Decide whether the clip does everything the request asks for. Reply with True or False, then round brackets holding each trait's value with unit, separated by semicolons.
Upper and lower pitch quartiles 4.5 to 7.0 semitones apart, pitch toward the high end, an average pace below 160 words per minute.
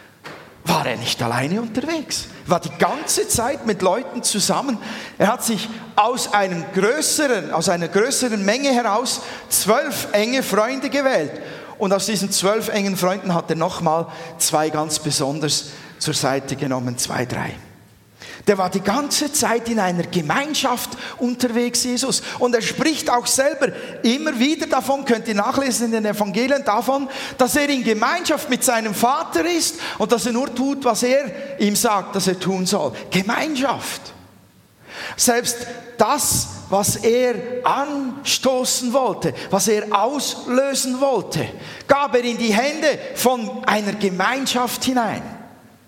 True (5.0 semitones; 235 Hz; 145 wpm)